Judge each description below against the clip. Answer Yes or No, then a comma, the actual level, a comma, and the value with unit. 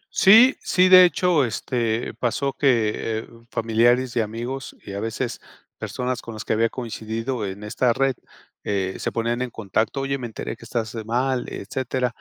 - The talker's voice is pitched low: Yes, low, 120 Hz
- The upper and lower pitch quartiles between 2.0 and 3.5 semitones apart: Yes, average, 2.8 semitones